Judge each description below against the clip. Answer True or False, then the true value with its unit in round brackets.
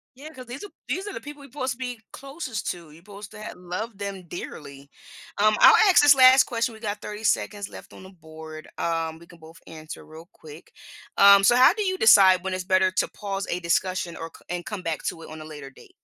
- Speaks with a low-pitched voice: False (195 Hz)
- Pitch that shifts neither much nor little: False (6.4 semitones)